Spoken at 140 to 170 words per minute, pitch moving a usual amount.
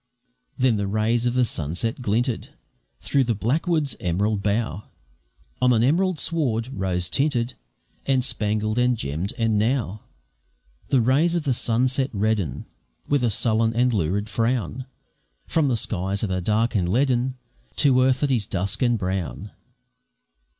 Yes: average, 150 wpm; average, 3.9 semitones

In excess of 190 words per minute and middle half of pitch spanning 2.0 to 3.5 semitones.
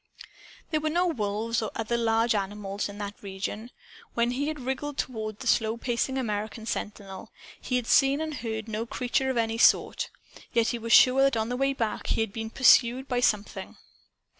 Yes: average, 200 wpm; average, 3.2 semitones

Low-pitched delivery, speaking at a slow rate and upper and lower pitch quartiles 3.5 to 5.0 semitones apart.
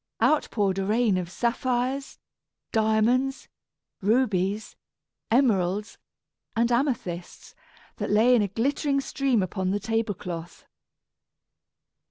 No: high, 220 Hz; slow, 105 wpm; average, 4.5 semitones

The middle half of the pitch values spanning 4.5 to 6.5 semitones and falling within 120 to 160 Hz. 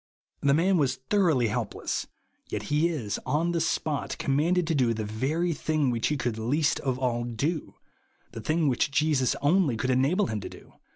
Yes: average, 4.8 semitones; medium, 140 Hz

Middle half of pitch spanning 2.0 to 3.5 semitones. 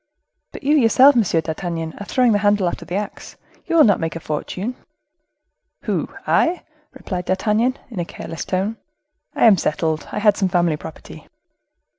No: average, 5.0 semitones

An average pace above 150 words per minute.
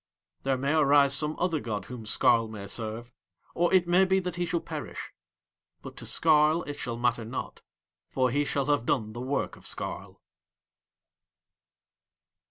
Yes: average, 165 wpm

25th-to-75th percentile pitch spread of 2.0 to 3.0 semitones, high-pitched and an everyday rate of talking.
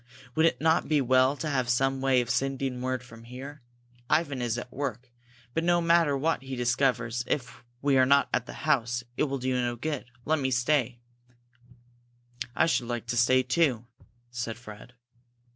No: average, 2.7 semitones; low, 130 Hz; average, 180 wpm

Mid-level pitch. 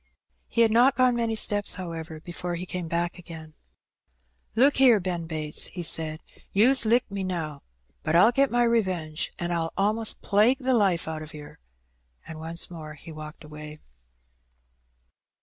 Yes: medium, 175 Hz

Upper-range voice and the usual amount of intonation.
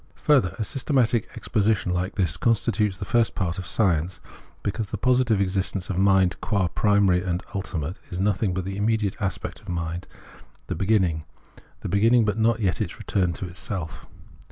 No: very low, 95 Hz; average, 3.2 semitones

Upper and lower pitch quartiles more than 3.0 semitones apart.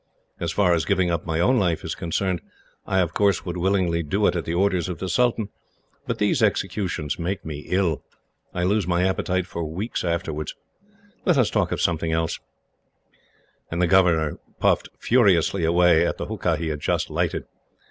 No: narrow, 2.5 semitones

